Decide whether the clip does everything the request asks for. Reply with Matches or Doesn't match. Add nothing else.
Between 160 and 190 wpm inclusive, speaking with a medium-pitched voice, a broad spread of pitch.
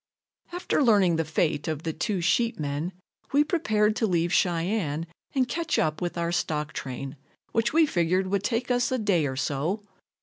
Matches